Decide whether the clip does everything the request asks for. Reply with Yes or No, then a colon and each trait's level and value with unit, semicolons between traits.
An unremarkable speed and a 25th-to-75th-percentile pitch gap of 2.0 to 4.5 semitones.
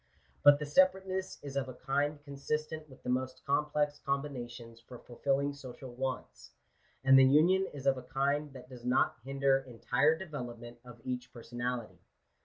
Yes: average, 160 wpm; average, 2.8 semitones